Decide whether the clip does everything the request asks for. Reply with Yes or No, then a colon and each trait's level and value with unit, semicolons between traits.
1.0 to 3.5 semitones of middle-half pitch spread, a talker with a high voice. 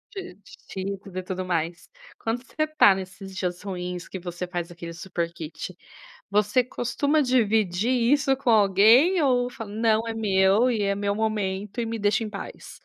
No: average, 4.0 semitones; high, 205 Hz